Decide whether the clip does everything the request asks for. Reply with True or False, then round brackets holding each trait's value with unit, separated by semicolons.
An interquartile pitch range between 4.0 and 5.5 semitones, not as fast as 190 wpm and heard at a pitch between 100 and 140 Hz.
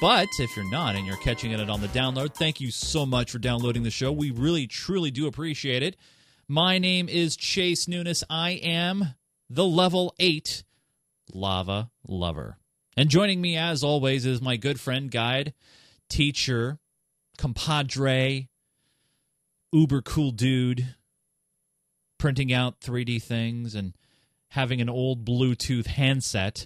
True (5.0 semitones; 140 wpm; 135 Hz)